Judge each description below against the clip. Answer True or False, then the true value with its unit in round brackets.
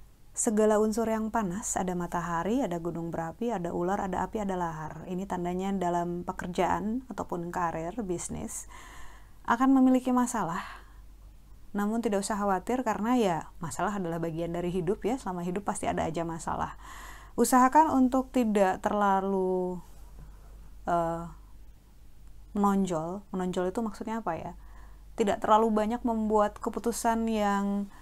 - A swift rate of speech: False (130 wpm)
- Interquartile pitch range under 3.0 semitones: False (4.4 semitones)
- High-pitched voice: True (195 Hz)